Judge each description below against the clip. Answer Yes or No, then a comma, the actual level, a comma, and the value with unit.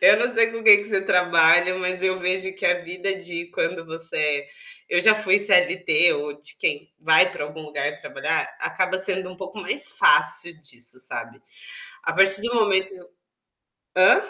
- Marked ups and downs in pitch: No, average, 3.3 semitones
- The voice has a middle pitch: Yes, medium, 180 Hz